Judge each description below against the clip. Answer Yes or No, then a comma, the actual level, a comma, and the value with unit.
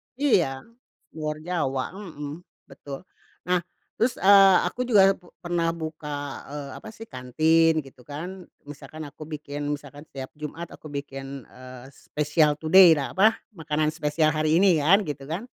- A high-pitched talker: No, medium, 155 Hz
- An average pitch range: Yes, average, 3.4 semitones